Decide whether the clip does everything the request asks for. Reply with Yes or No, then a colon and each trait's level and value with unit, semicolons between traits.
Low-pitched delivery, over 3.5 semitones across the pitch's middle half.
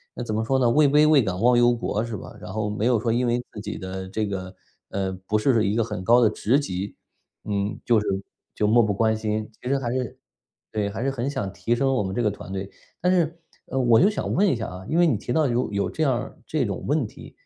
Yes: low, 115 Hz; average, 3.9 semitones